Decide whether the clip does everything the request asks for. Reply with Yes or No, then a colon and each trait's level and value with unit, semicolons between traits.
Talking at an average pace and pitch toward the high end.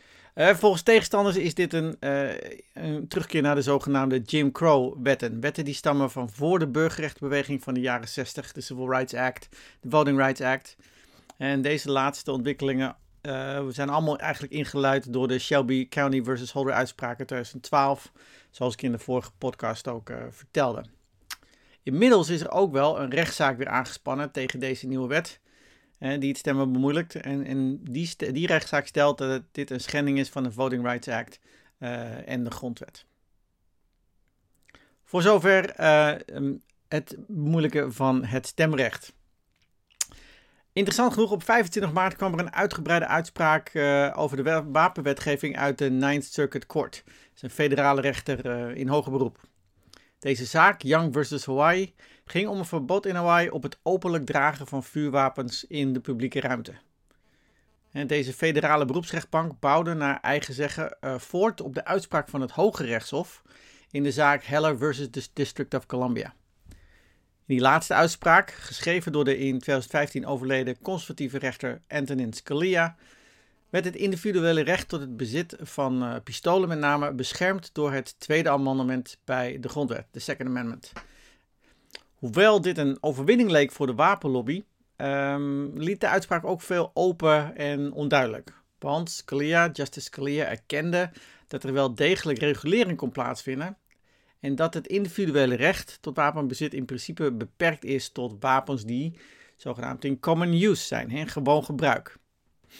No: average, 155 wpm; medium, 140 Hz